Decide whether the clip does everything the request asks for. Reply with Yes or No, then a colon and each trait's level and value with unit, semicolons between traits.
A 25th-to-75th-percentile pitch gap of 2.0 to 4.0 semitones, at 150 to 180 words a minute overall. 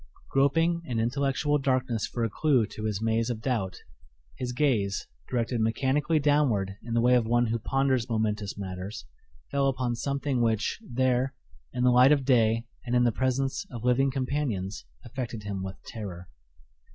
Yes: average, 3.4 semitones; average, 165 wpm